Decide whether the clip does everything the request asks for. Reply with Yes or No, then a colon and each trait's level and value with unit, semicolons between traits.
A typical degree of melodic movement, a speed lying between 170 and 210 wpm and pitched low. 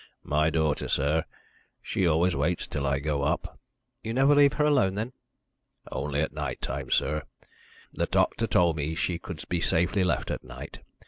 Yes: average, 4.2 semitones; average, 175 wpm; very low, 80 Hz